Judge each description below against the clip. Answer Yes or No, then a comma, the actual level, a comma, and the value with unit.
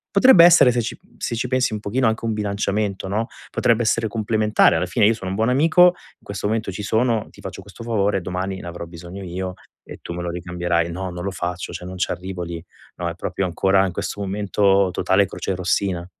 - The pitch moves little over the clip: No, average, 3.7 semitones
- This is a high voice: No, low, 100 Hz